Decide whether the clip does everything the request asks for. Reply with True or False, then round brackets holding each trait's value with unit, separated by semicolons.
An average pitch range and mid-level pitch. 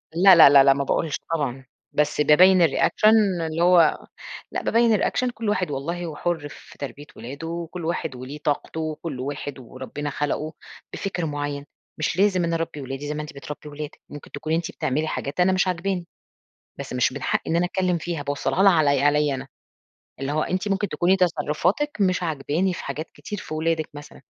True (3.6 semitones; 160 Hz)